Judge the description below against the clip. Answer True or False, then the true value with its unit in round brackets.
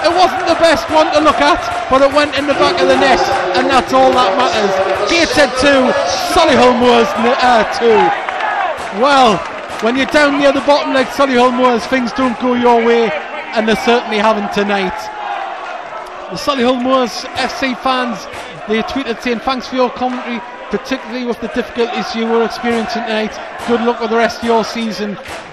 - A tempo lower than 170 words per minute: False (185 wpm)